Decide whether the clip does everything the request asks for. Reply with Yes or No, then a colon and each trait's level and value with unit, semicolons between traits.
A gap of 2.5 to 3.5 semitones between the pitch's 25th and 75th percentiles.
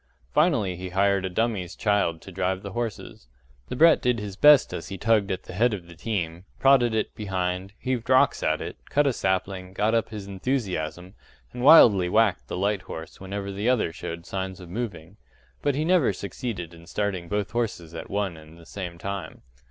No: average, 4.1 semitones